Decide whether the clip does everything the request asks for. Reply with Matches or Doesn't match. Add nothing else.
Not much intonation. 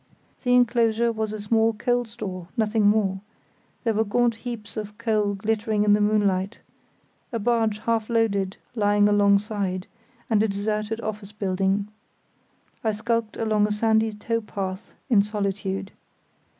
Matches